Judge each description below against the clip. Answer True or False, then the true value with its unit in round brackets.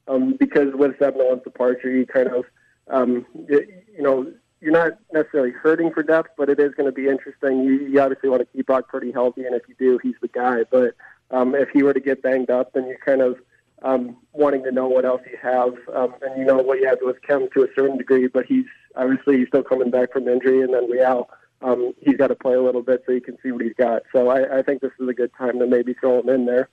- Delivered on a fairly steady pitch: True (1.5 semitones)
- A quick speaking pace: True (265 wpm)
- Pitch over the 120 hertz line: True (130 Hz)